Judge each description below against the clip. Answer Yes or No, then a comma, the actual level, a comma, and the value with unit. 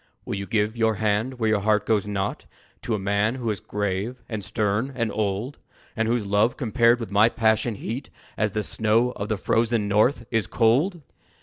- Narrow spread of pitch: Yes, narrow, 2.3 semitones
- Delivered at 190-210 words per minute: Yes, average, 195 wpm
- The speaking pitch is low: Yes, low, 110 Hz